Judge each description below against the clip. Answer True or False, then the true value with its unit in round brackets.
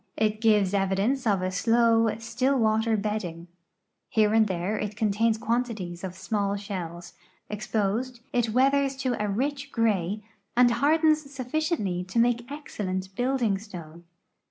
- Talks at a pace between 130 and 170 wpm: True (140 wpm)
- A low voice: False (220 Hz)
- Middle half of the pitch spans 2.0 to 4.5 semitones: True (3.9 semitones)